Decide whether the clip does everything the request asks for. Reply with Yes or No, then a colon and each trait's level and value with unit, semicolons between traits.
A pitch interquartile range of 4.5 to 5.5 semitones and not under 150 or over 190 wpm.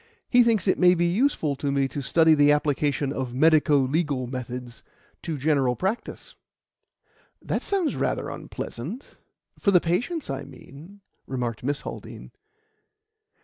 No: average, 5.1 semitones; average, 140 wpm